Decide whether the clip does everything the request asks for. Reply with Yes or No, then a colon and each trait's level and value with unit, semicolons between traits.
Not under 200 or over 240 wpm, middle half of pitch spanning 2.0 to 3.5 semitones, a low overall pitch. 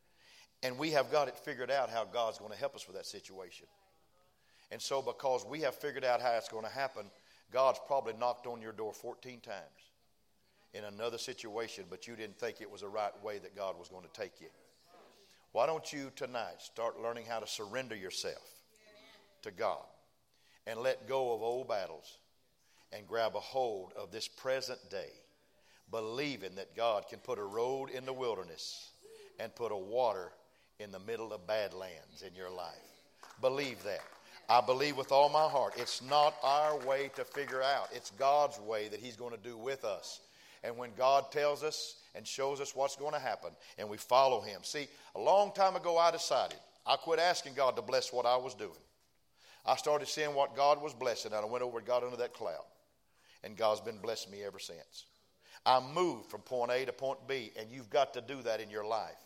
No: fast, 205 wpm; average, 4.2 semitones; low, 130 Hz